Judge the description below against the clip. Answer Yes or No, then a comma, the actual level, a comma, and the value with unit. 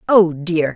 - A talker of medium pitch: Yes, medium, 175 Hz